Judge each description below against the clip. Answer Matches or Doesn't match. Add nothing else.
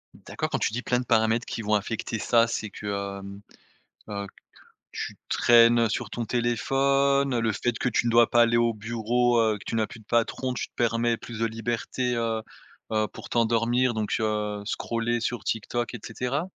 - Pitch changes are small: Matches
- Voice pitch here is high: Doesn't match